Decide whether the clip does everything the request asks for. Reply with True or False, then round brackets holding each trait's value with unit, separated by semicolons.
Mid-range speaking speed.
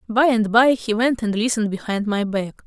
False (225 wpm)